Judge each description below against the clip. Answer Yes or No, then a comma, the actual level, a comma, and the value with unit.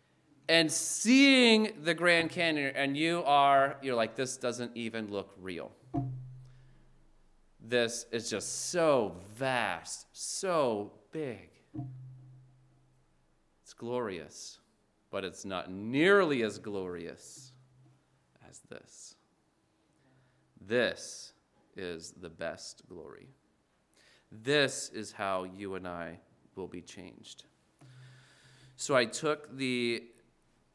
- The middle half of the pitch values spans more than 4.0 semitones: Yes, average, 5.3 semitones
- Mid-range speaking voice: No, low, 130 Hz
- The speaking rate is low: Yes, slow, 100 wpm